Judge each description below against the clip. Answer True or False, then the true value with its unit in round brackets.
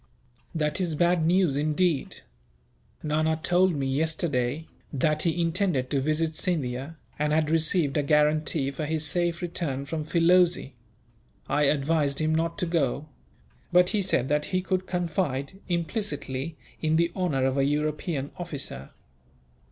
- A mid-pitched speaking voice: True (155 Hz)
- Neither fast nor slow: True (145 wpm)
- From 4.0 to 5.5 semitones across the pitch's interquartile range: False (3.2 semitones)